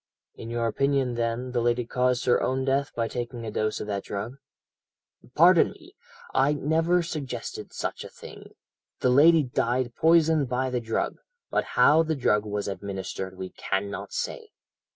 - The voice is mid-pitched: No, low, 125 Hz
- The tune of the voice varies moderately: Yes, average, 4.0 semitones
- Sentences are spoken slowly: No, average, 165 wpm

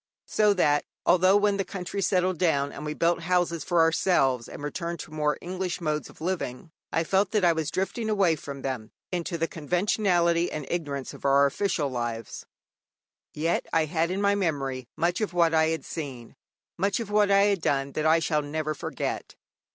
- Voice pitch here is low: No, medium, 165 Hz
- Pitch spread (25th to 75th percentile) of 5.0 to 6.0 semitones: No, average, 3.9 semitones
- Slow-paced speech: No, average, 190 wpm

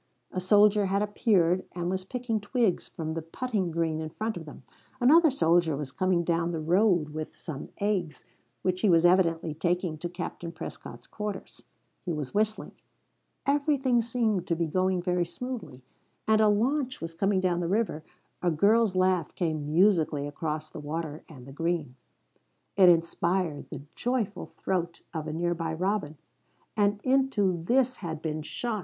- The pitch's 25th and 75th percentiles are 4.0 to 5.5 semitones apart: Yes, average, 4.4 semitones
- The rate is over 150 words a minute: Yes, average, 165 wpm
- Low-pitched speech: No, medium, 180 Hz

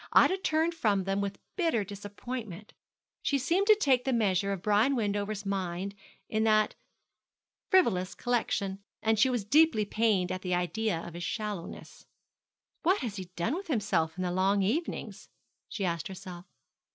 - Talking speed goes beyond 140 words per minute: Yes, average, 160 wpm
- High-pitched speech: Yes, high, 205 Hz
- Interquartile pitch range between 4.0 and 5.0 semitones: Yes, average, 4.4 semitones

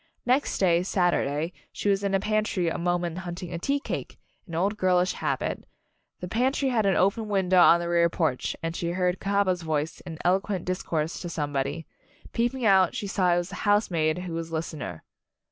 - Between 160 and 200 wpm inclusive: Yes, average, 190 wpm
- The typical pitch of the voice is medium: Yes, medium, 180 Hz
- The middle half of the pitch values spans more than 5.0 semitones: No, average, 3.0 semitones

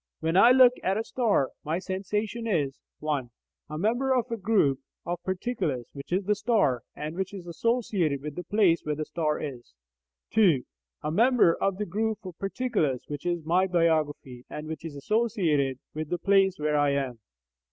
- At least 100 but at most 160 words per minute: No, average, 185 wpm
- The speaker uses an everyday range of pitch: No, wide, 5.8 semitones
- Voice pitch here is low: No, medium, 175 Hz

